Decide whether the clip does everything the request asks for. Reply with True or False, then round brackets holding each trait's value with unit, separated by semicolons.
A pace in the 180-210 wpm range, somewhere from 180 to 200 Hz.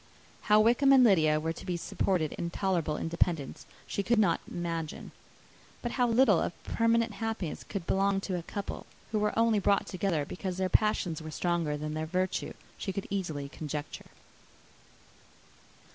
False (160 wpm; 185 Hz)